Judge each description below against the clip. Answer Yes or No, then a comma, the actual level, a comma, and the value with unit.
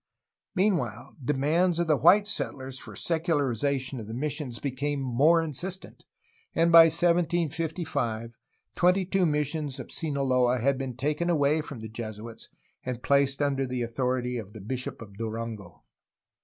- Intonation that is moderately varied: Yes, average, 5.0 semitones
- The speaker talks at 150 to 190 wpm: No, average, 140 wpm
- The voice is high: No, medium, 140 Hz